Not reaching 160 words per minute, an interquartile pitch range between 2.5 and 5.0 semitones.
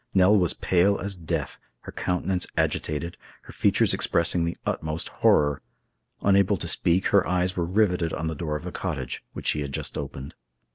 No: average, 180 wpm; average, 3.0 semitones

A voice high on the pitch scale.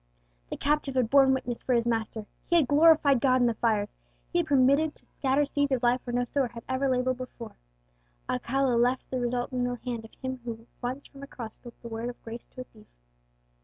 Yes: very high, 255 Hz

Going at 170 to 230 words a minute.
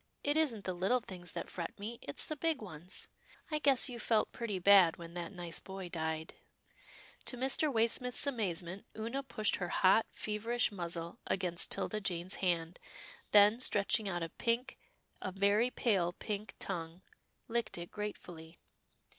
No: average, 160 wpm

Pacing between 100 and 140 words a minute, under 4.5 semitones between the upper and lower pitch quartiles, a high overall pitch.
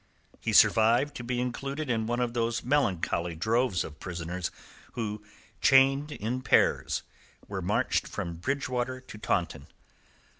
No: slow, 135 wpm; average, 3.9 semitones; low, 120 Hz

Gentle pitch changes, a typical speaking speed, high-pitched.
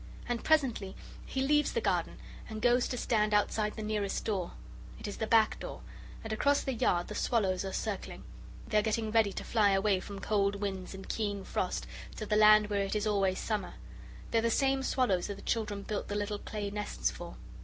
No: narrow, 2.1 semitones; fast, 210 wpm; high, 210 Hz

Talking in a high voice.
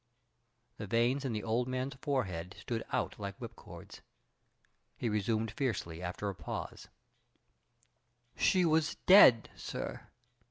No: low, 115 Hz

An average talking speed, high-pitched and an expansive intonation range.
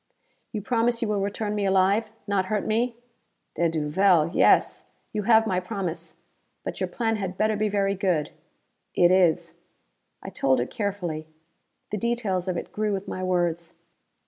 No: average, 165 wpm; high, 195 Hz; average, 3.4 semitones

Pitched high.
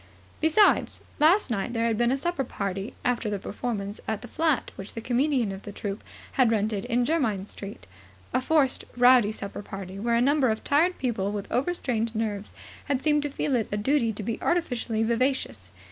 Yes: high, 235 Hz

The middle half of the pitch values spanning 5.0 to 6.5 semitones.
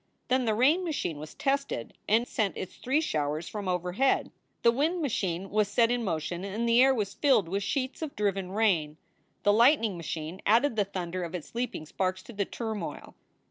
Yes: wide, 5.4 semitones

